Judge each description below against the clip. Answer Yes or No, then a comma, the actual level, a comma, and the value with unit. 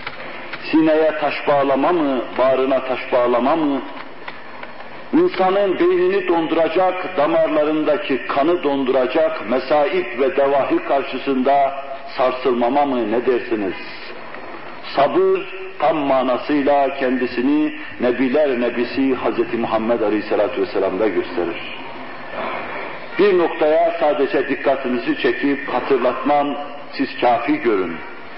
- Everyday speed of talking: No, slow, 90 wpm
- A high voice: No, medium, 150 Hz